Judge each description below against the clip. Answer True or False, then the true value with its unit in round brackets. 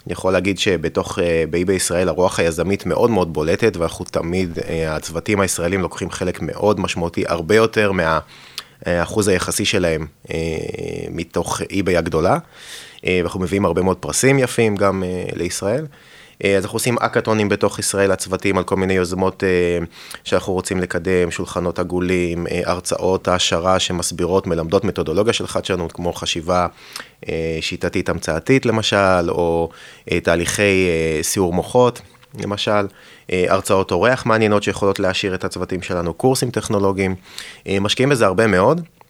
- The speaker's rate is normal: True (125 wpm)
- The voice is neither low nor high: False (95 Hz)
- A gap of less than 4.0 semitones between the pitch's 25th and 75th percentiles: True (2.7 semitones)